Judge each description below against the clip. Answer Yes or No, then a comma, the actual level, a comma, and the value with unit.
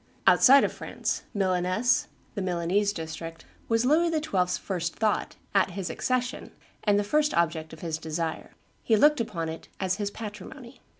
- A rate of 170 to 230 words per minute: No, average, 160 wpm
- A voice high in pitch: Yes, high, 200 Hz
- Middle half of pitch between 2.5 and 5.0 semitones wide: No, wide, 5.4 semitones